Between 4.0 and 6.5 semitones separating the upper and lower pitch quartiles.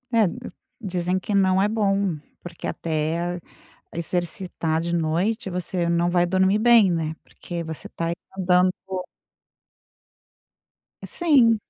No: narrow, 2.6 semitones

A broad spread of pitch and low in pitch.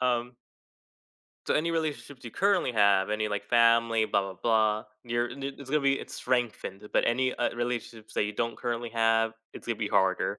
No: average, 2.7 semitones; low, 115 Hz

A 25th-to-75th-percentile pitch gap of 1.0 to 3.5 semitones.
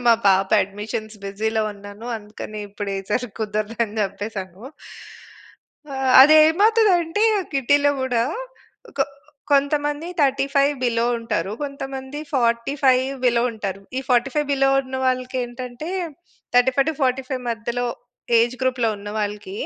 No: average, 4.3 semitones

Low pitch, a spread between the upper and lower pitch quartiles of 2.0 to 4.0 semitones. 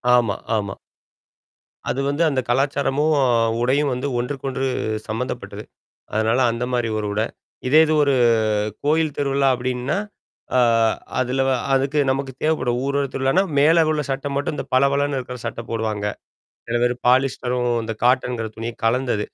Yes: low, 130 Hz; narrow, 2.5 semitones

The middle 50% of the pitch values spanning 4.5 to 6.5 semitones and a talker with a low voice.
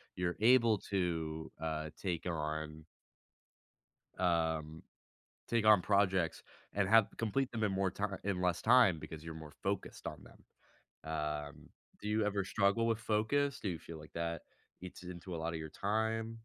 Yes: average, 5.0 semitones; very low, 90 Hz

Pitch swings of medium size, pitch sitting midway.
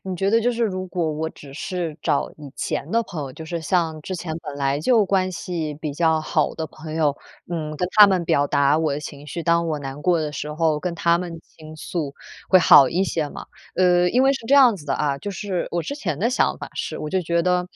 Yes: average, 3.5 semitones; medium, 165 Hz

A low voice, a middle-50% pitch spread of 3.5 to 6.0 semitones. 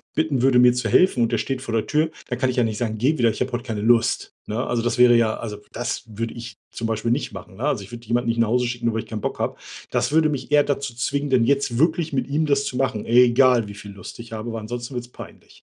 No: low, 120 Hz; average, 2.7 semitones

